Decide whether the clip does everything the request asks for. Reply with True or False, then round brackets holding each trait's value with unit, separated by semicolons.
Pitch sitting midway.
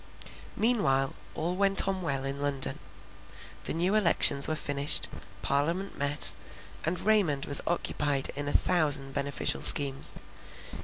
True (145 Hz)